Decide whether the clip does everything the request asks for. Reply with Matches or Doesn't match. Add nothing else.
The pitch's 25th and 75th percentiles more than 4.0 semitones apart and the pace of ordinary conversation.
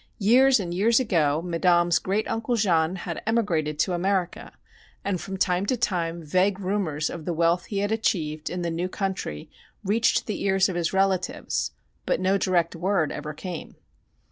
Doesn't match